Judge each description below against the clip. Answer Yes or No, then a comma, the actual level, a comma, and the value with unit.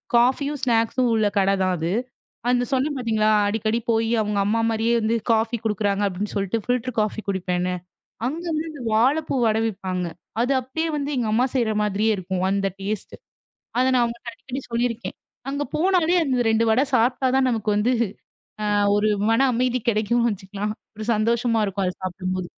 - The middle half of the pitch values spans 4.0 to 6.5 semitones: No, average, 3.4 semitones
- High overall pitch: Yes, high, 225 Hz